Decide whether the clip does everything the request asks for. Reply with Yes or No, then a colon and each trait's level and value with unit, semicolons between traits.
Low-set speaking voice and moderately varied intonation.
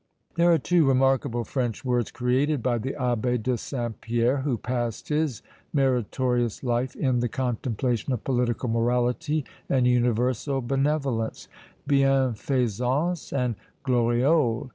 No: low, 125 Hz; narrow, 2.2 semitones